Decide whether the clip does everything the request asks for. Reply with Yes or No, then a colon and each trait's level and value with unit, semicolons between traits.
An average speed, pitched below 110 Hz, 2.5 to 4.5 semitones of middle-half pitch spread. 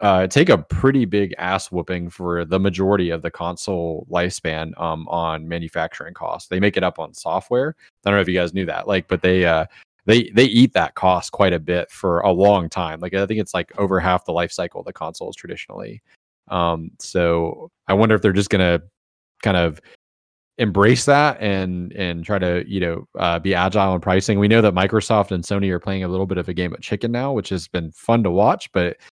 No: fast, 225 wpm; very low, 90 Hz; average, 2.9 semitones